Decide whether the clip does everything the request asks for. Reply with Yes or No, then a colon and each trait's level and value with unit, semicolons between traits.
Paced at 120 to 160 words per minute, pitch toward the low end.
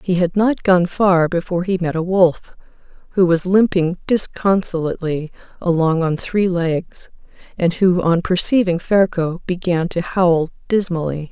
No: average, 145 wpm; medium, 175 Hz